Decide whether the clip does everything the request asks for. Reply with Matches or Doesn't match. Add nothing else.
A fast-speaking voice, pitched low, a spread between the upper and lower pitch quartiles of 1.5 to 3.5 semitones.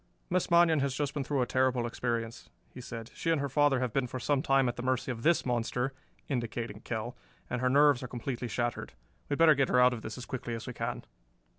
Matches